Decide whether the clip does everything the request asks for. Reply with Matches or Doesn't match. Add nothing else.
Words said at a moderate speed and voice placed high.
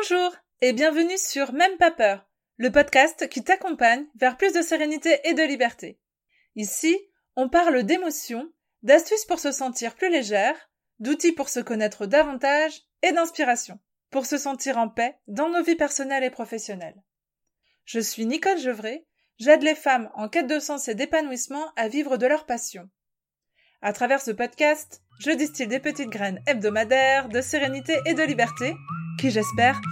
Matches